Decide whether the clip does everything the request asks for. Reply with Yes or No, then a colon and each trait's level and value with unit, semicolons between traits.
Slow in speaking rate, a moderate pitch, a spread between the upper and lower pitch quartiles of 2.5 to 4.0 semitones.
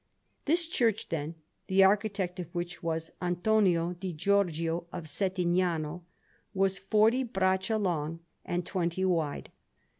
Yes: slow, 120 wpm; medium, 180 Hz; average, 2.8 semitones